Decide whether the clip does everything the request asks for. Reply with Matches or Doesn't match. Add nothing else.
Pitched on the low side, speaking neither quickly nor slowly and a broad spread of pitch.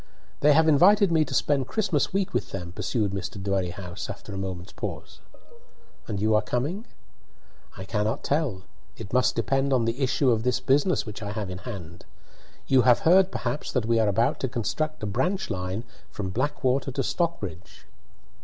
Matches